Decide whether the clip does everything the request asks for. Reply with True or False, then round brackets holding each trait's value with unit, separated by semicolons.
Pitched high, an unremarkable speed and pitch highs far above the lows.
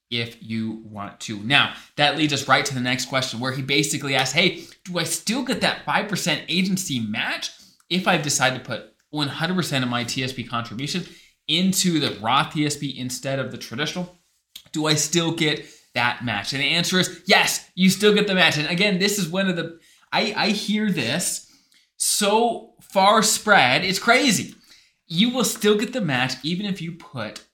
False (160 Hz; 195 wpm; 6.2 semitones)